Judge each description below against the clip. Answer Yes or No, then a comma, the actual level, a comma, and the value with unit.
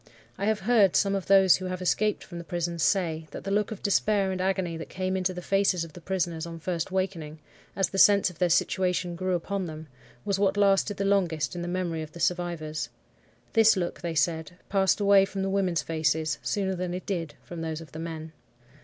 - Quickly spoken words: Yes, fast, 225 wpm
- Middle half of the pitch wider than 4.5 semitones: No, average, 2.8 semitones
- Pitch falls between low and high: Yes, medium, 180 Hz